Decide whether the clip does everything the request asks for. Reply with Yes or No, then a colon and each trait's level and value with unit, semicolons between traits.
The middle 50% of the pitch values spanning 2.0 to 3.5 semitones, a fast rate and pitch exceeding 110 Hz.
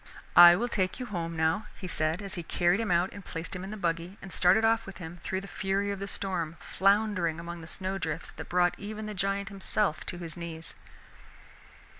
Yes: average, 2.8 semitones; fast, 220 wpm; medium, 185 Hz